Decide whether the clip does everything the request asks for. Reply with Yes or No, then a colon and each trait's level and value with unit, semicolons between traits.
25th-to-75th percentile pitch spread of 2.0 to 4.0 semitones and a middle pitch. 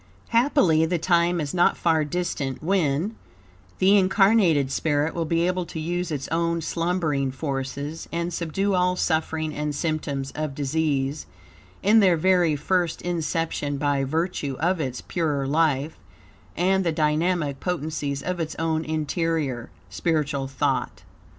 Yes: average, 3.3 semitones; medium, 160 Hz